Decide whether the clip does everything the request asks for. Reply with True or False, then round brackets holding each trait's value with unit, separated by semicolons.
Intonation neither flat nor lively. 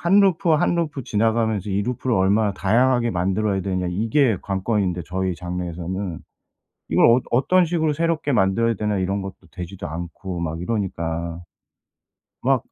True (4.9 semitones)